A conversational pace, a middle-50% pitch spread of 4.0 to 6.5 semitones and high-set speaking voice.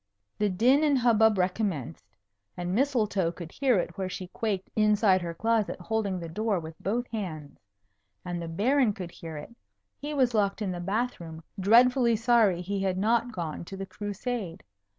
Yes: average, 175 wpm; average, 4.5 semitones; high, 200 Hz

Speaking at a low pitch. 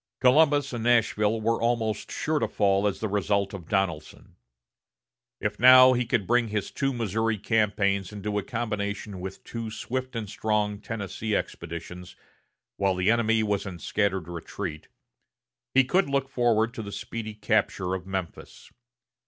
Yes: low, 105 Hz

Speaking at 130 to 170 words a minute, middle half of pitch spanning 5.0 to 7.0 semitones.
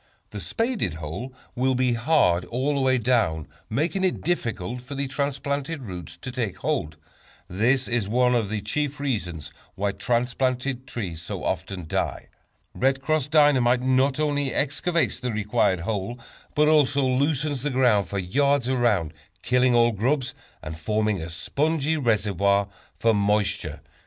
Yes: average, 150 wpm; wide, 5.4 semitones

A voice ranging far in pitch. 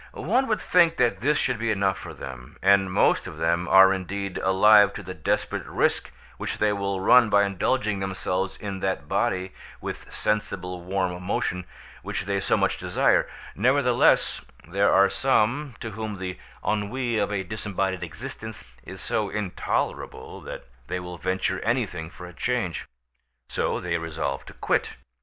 No: average, 3.0 semitones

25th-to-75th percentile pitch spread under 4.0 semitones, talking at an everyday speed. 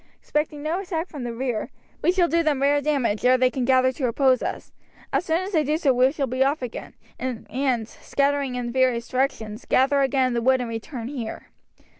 No: average, 2.8 semitones; fast, 215 wpm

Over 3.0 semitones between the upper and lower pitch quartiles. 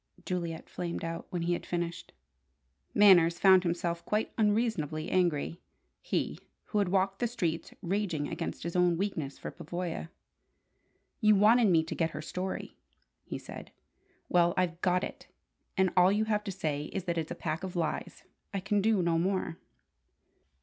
No: average, 2.7 semitones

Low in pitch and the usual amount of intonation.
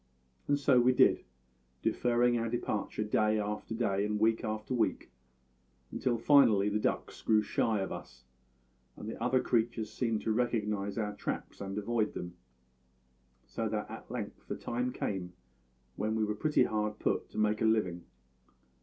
No: low, 110 Hz; narrow, 2.1 semitones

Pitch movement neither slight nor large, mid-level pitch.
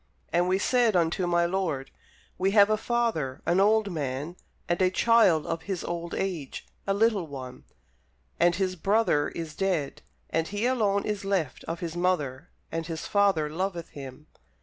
Yes: average, 3.8 semitones; medium, 175 Hz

